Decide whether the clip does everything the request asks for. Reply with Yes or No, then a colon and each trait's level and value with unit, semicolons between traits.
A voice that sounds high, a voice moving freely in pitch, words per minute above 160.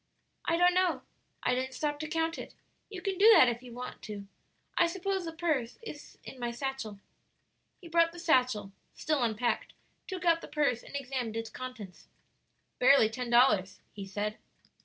Yes: very high, 260 Hz; wide, 6.1 semitones; average, 180 wpm